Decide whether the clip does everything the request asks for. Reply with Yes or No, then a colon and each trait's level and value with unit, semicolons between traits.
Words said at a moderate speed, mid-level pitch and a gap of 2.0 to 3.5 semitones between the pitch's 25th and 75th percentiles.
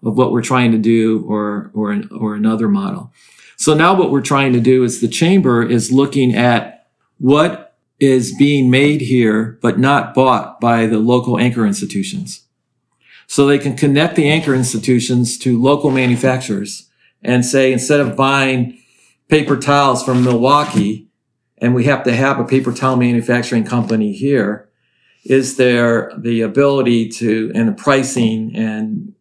No: average, 155 wpm; low, 125 Hz; average, 3.0 semitones